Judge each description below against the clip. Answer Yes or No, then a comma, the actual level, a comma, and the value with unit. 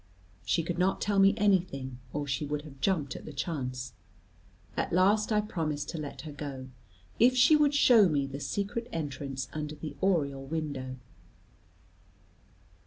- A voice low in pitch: No, medium, 155 Hz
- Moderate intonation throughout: No, wide, 6.0 semitones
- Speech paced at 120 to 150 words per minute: No, average, 160 wpm